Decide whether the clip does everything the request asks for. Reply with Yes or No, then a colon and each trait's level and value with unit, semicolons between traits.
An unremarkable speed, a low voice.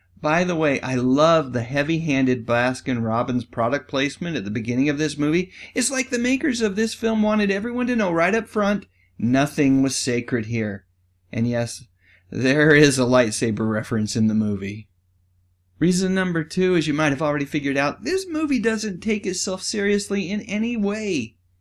No: average, 180 wpm; medium, 145 Hz